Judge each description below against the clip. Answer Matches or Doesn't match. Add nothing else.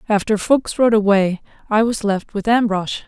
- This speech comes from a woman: Matches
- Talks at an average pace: Matches